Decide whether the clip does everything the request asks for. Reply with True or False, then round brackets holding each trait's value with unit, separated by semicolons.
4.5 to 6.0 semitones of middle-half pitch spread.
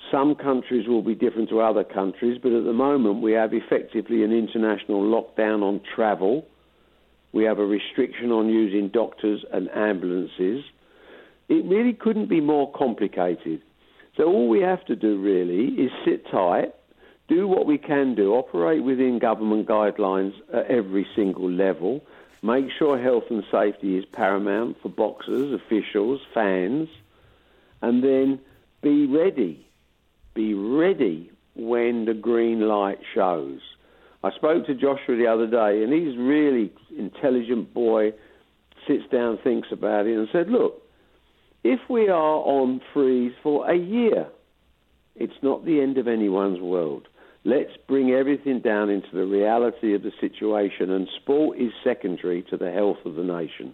True (5.1 semitones)